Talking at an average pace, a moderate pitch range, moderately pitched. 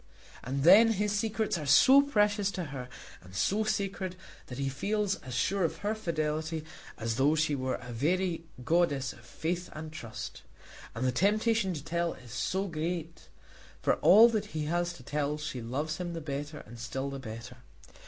No: average, 185 wpm; wide, 6.1 semitones; medium, 160 Hz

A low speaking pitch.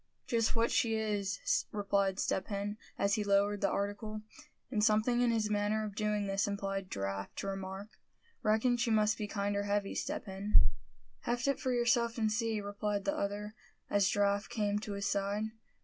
No: high, 205 Hz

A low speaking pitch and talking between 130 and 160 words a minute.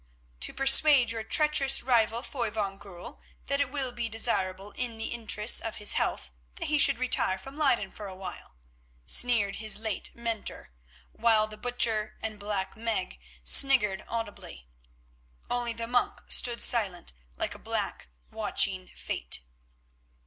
No: high, 225 Hz; average, 150 wpm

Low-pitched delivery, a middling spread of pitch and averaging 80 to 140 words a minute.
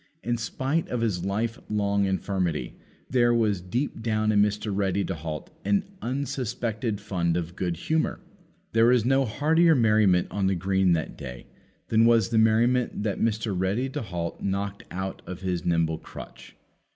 No: low, 105 Hz; average, 3.9 semitones; average, 165 wpm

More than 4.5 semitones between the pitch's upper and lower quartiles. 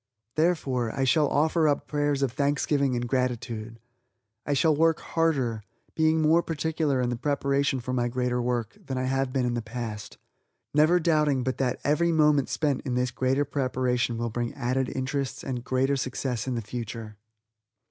No: average, 3.1 semitones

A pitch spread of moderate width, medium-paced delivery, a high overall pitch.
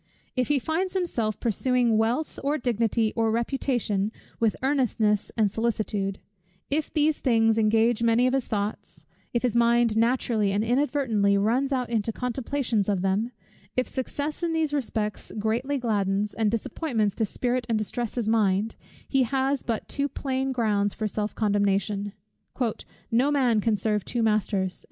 Yes: average, 3.6 semitones; average, 150 wpm; high, 230 Hz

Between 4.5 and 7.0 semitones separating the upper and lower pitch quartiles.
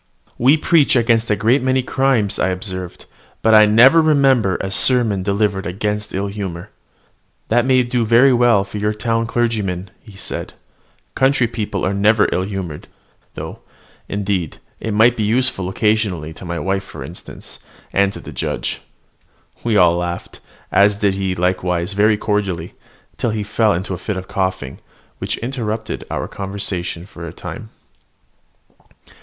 No: average, 3.6 semitones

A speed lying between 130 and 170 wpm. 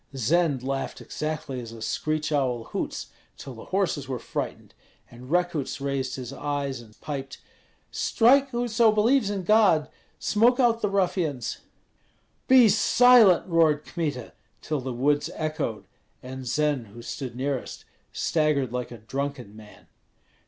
Yes: average, 140 wpm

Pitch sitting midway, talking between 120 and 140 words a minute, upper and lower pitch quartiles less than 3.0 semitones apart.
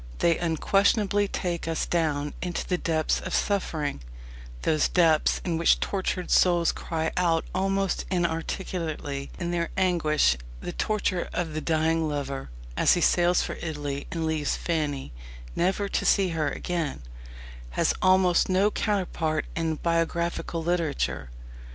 Yes: medium, 170 Hz; slow, 135 wpm; narrow, 2.5 semitones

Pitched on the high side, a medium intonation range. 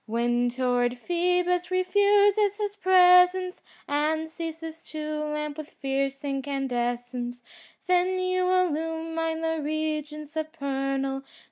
Yes: very high, 315 Hz; average, 4.8 semitones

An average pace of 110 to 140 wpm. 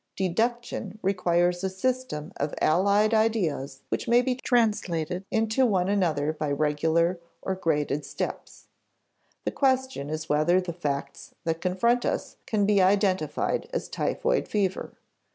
Yes: slow, 135 wpm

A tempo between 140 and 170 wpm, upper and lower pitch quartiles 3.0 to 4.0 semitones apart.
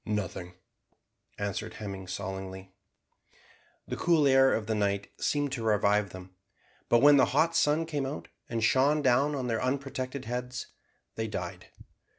No: average, 150 wpm; wide, 5.6 semitones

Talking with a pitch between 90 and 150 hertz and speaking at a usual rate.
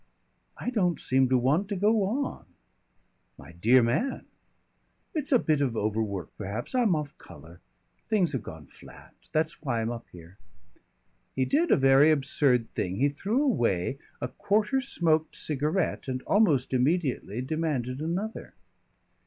Yes: medium, 140 Hz; average, 145 wpm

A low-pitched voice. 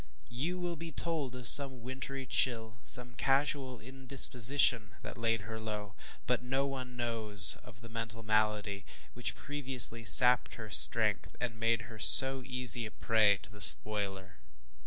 Yes: low, 120 Hz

